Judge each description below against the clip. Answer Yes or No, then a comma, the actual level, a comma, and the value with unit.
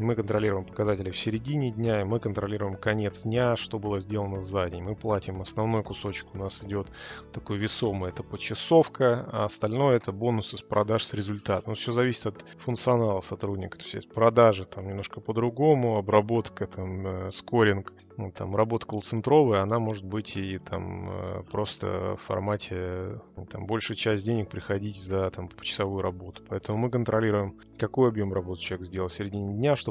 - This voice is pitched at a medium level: No, low, 105 Hz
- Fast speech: Yes, fast, 170 wpm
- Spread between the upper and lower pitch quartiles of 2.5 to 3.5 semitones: Yes, average, 2.8 semitones